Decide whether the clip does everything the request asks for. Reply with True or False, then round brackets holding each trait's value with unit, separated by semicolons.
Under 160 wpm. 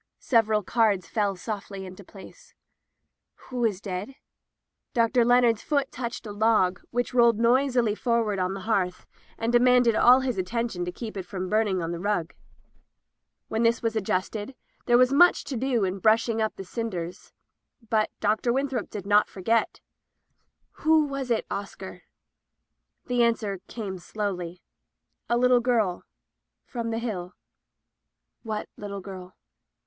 True (150 wpm)